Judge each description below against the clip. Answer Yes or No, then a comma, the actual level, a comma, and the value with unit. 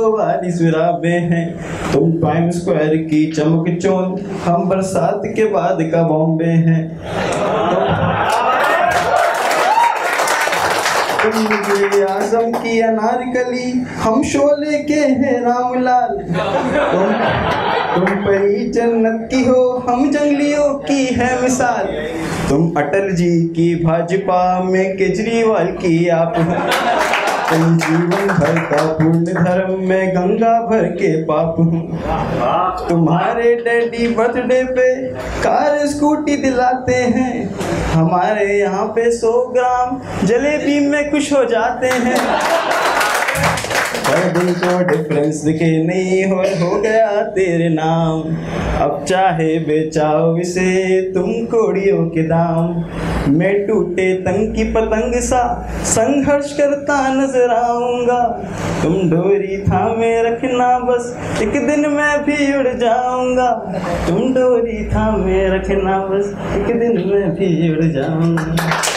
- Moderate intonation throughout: No, wide, 6.3 semitones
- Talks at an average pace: No, slow, 105 wpm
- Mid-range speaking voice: No, high, 195 Hz